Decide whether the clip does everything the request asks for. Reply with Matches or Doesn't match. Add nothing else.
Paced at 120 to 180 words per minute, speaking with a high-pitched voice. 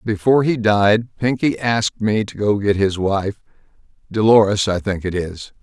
Doesn't match